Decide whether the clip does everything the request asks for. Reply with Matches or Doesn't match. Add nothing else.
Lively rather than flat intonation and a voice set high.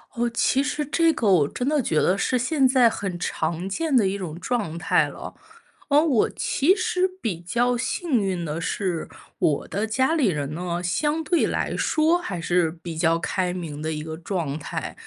Matches